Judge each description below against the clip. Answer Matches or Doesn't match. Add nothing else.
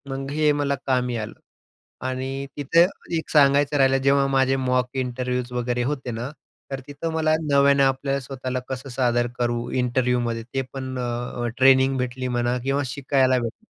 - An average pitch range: Doesn't match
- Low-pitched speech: Matches